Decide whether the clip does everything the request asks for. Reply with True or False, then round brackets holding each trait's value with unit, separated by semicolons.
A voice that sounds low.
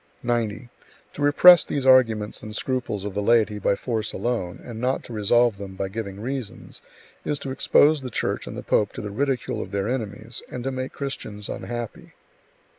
True (115 Hz)